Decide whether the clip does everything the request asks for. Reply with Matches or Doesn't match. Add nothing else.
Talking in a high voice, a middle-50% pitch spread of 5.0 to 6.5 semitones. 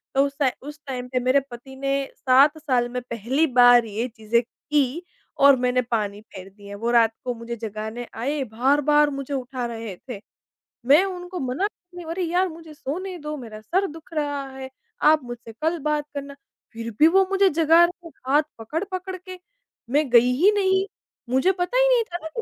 Matches